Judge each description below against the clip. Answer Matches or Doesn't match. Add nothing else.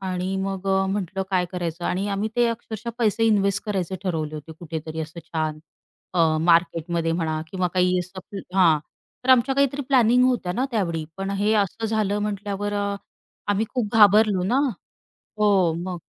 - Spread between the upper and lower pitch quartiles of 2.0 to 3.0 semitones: Doesn't match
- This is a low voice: Doesn't match